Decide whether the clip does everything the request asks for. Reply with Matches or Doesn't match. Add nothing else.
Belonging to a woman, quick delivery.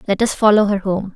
Matches